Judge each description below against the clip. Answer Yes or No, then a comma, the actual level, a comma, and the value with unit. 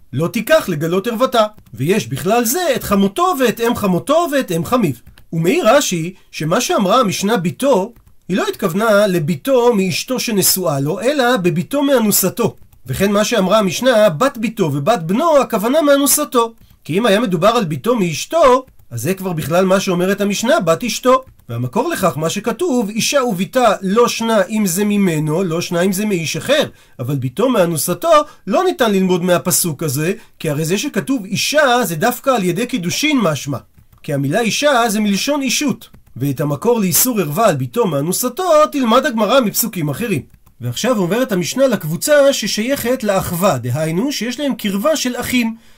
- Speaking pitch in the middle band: No, high, 205 Hz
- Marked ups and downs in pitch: Yes, wide, 6.2 semitones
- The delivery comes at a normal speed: No, fast, 160 wpm